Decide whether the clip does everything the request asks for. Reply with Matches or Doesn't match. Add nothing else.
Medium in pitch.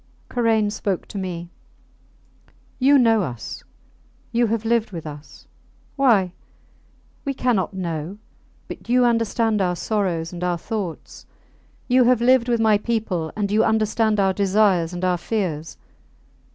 Doesn't match